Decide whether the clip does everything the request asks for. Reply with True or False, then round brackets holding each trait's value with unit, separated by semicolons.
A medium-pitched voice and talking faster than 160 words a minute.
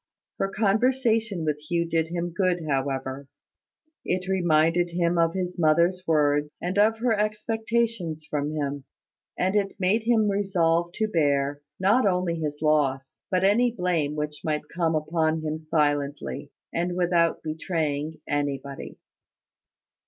False (170 Hz; 135 wpm)